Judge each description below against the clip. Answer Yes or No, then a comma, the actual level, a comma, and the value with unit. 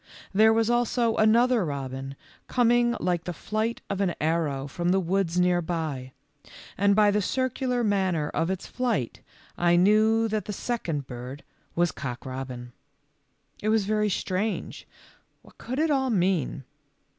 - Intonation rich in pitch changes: Yes, wide, 5.8 semitones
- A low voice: No, high, 190 Hz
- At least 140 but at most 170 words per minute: Yes, average, 150 wpm